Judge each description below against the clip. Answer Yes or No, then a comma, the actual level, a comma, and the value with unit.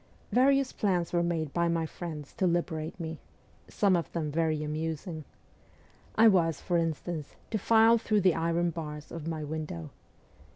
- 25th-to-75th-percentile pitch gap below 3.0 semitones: Yes, narrow, 2.5 semitones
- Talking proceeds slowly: No, average, 160 wpm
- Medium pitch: Yes, medium, 165 Hz